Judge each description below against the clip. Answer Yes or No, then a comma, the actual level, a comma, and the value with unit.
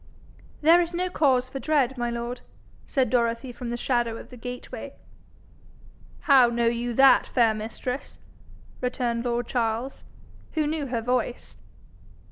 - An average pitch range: No, narrow, 2.2 semitones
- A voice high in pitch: Yes, high, 245 Hz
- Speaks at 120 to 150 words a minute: Yes, average, 140 wpm